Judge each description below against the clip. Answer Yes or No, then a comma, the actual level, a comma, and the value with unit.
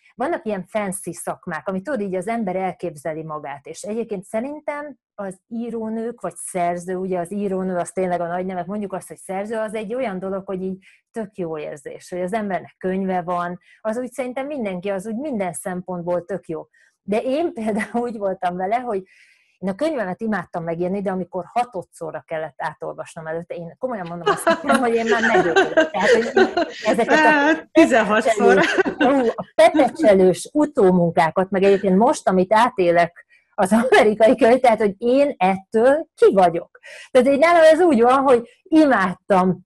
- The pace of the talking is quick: Yes, fast, 160 wpm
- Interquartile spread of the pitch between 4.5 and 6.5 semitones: Yes, wide, 5.6 semitones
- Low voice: No, high, 200 Hz